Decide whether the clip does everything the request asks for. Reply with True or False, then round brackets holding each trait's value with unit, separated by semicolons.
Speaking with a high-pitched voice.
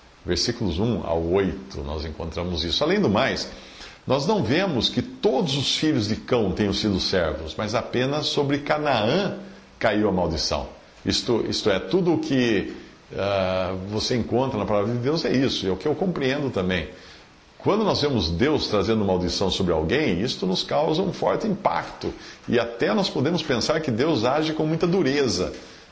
False (105 Hz)